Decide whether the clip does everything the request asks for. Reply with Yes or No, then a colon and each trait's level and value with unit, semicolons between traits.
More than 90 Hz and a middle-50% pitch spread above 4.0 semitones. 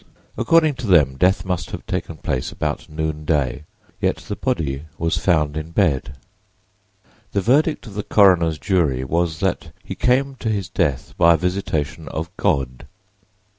No: very low, 85 Hz; average, 4.7 semitones